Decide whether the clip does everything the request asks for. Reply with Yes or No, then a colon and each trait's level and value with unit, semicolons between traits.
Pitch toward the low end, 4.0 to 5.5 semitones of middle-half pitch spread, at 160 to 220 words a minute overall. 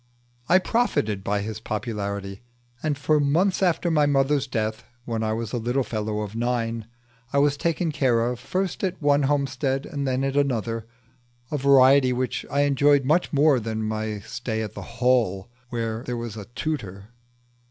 Yes: low, 125 Hz; average, 4.4 semitones; average, 175 wpm